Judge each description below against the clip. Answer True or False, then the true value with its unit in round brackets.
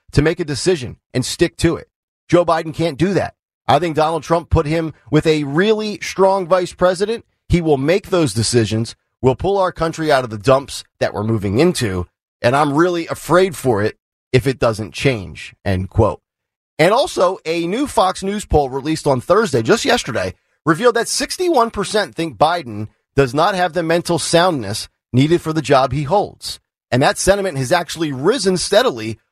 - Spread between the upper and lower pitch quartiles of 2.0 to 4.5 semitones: False (5.6 semitones)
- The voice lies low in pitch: False (160 Hz)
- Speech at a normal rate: True (185 wpm)